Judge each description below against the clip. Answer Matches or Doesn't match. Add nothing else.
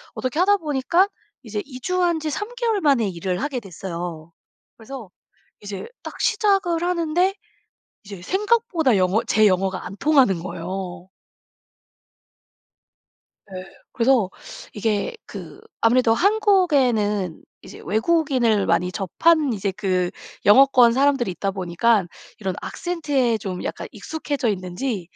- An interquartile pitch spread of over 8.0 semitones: Matches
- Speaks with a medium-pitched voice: Doesn't match